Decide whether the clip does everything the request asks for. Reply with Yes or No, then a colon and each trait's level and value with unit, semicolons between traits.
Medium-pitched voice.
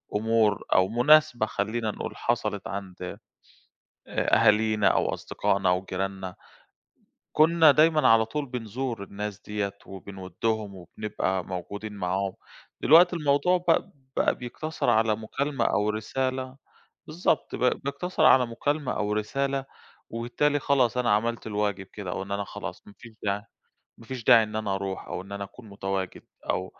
No: low, 110 Hz